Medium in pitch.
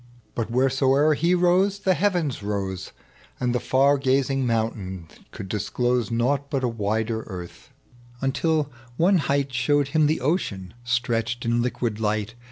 No: low, 125 Hz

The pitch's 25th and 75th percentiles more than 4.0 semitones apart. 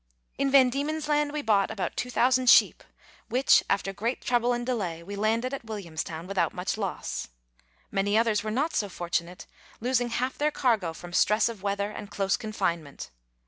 Yes: average, 4.4 semitones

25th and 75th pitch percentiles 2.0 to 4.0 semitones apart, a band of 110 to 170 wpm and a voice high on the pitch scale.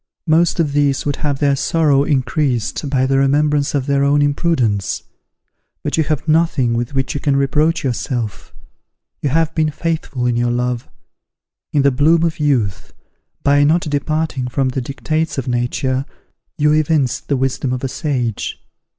No: average, 2.9 semitones; average, 165 wpm; medium, 140 Hz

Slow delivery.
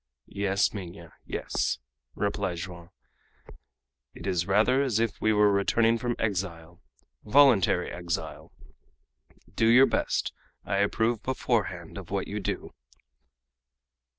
Yes: slow, 115 wpm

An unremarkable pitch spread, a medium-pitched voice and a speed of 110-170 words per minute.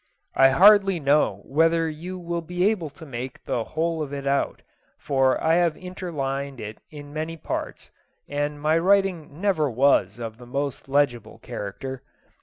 Yes: average, 3.9 semitones; medium, 150 Hz; average, 160 wpm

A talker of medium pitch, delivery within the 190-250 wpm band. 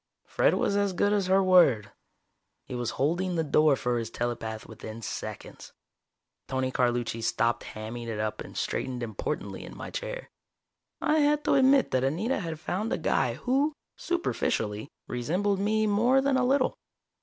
No: medium, 165 Hz; average, 165 wpm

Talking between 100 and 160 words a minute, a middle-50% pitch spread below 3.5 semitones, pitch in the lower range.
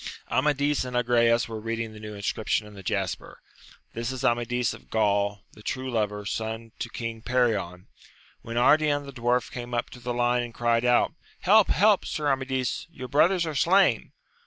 No: average, 185 wpm; average, 2.9 semitones; low, 120 Hz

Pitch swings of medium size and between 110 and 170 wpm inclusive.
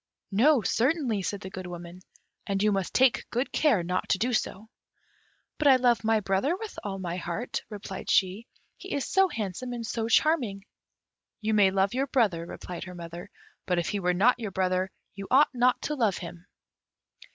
No: average, 4.9 semitones; average, 190 wpm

